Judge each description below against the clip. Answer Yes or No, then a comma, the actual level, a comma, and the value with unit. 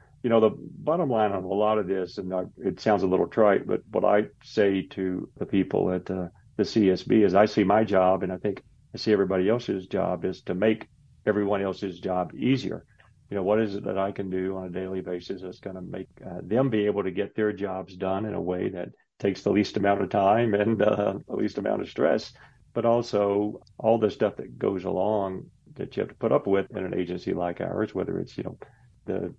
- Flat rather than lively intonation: Yes, narrow, 2.3 semitones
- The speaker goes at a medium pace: No, fast, 235 wpm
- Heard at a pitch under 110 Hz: Yes, low, 100 Hz